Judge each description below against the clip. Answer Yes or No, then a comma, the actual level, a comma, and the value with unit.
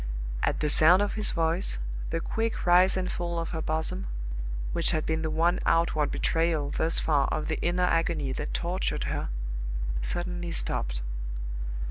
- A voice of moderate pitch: Yes, medium, 165 Hz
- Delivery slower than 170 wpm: Yes, average, 160 wpm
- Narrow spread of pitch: Yes, narrow, 2.1 semitones